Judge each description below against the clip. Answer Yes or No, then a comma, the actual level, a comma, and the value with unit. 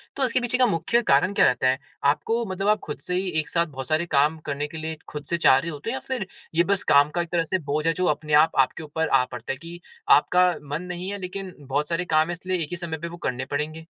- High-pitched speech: No, medium, 165 Hz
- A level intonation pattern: No, average, 3.7 semitones